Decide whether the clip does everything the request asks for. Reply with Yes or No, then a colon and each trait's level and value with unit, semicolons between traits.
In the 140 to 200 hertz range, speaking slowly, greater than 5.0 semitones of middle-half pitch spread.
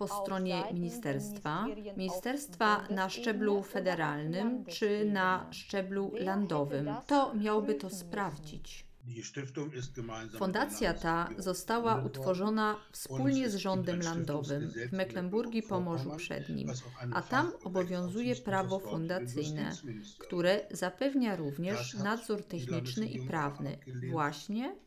Yes: medium, 185 Hz; slow, 95 wpm; wide, 5.6 semitones